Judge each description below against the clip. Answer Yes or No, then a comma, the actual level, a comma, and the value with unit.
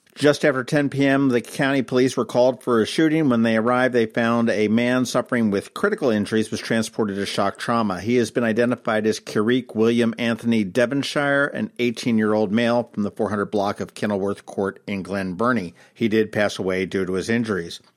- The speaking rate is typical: Yes, average, 195 wpm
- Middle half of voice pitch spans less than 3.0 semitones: Yes, narrow, 2.6 semitones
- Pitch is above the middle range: No, low, 115 Hz